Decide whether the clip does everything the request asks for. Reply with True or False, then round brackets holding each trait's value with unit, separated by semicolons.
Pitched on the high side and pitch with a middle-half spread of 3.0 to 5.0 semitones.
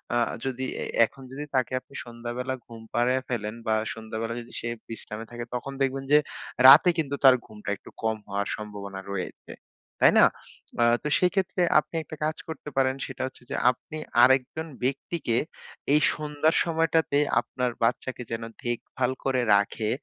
False (125 Hz; 3.8 semitones)